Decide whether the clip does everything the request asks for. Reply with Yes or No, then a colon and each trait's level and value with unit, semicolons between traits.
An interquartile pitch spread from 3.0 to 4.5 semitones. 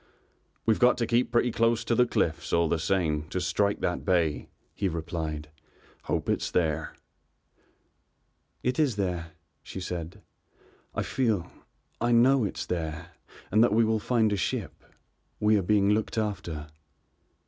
No: wide, 5.5 semitones